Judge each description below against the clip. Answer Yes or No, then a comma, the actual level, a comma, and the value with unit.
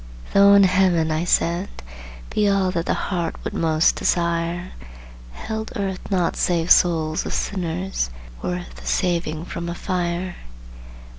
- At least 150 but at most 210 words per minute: No, average, 140 wpm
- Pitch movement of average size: No, narrow, 2.0 semitones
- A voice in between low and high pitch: Yes, medium, 175 Hz